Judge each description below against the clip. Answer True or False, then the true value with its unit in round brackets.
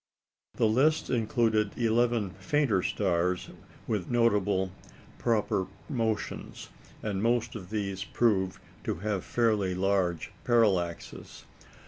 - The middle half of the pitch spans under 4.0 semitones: True (3.5 semitones)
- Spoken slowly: True (100 wpm)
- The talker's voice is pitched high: False (105 Hz)